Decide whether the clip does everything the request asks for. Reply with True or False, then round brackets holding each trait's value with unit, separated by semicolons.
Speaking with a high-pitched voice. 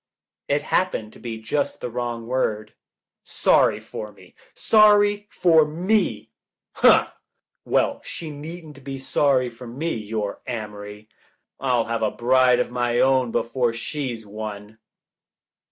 False (125 Hz)